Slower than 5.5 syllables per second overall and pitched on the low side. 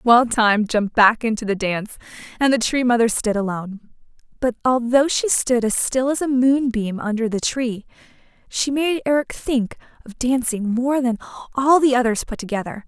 No: 5.1 syllables/s; high, 240 Hz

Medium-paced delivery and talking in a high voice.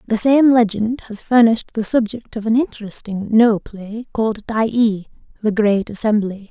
Yes: average, 165 wpm; high, 220 Hz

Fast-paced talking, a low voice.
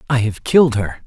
Yes: fast, 225 wpm; low, 120 Hz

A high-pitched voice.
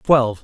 No: low, 125 Hz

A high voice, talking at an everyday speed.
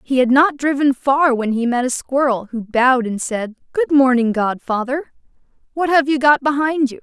Yes: very high, 265 Hz; average, 195 wpm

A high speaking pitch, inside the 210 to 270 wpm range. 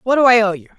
No: high, 225 Hz; fast, 385 wpm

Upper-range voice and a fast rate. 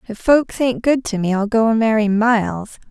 Yes: high, 225 Hz; fast, 225 wpm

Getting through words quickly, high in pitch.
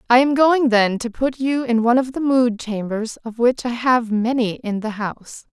Yes: fast, 225 wpm; high, 240 Hz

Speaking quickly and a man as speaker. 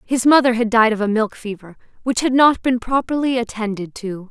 No: fast, 210 wpm; female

